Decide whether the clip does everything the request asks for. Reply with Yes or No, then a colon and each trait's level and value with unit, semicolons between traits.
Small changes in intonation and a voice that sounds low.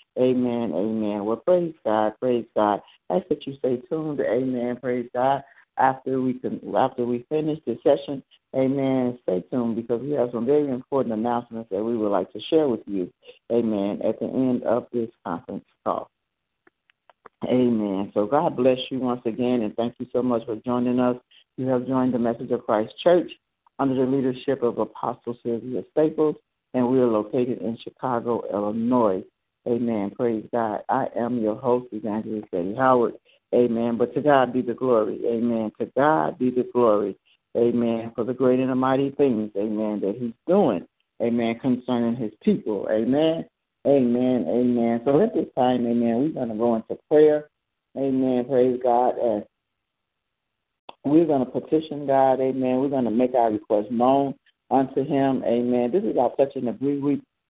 Yes: narrow, 2.2 semitones; low, 125 Hz